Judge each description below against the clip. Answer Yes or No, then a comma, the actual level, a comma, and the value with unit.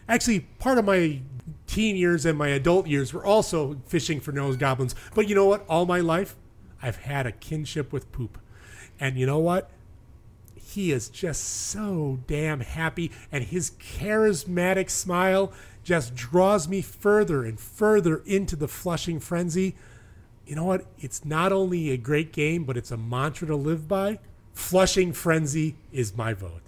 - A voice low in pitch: No, medium, 155 Hz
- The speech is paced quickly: No, average, 165 wpm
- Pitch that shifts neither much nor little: No, wide, 6.1 semitones